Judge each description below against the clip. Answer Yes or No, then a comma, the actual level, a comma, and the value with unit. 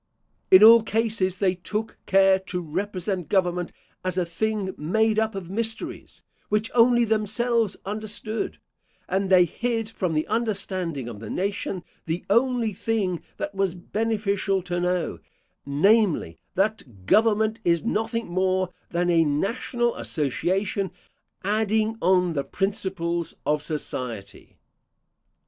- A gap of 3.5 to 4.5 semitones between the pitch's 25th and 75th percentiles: Yes, average, 3.8 semitones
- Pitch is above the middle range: Yes, high, 195 Hz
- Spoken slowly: Yes, slow, 125 wpm